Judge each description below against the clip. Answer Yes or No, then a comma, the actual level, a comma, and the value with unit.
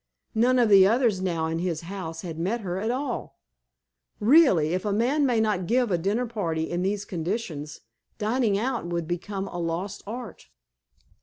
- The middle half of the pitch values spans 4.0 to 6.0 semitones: Yes, average, 5.0 semitones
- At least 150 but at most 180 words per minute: Yes, average, 170 wpm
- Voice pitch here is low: No, high, 195 Hz